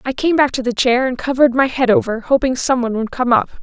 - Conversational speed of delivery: No, fast, 280 wpm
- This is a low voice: No, very high, 255 Hz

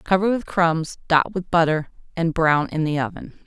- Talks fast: No, average, 190 wpm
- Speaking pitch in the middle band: Yes, medium, 165 Hz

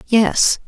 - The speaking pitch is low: No, high, 215 Hz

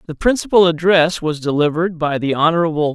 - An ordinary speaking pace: Yes, average, 165 wpm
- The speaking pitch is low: No, medium, 165 Hz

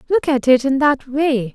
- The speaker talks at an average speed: No, fast, 235 wpm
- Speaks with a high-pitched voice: Yes, very high, 270 Hz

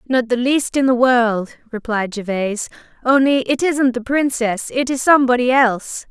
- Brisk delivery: No, average, 155 wpm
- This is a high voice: Yes, high, 245 Hz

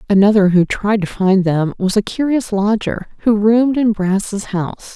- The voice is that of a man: No, female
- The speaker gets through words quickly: No, average, 180 wpm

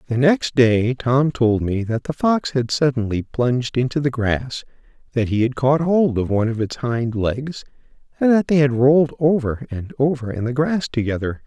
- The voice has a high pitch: No, low, 130 Hz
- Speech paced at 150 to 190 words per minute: No, average, 200 wpm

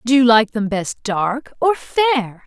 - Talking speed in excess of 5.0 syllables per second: No, 4.4 syllables/s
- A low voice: No, high, 240 Hz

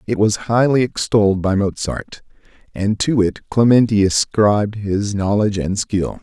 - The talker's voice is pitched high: No, low, 105 Hz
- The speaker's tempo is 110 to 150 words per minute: Yes, average, 145 wpm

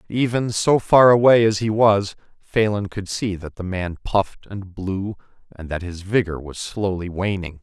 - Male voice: Yes, male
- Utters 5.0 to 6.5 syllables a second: No, 4.5 syllables/s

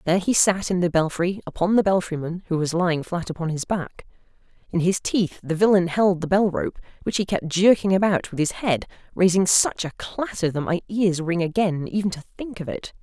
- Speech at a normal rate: No, fast, 220 wpm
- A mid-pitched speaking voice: Yes, medium, 180 Hz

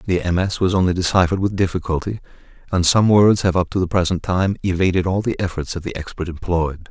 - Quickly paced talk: Yes, fast, 210 wpm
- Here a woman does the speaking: No, male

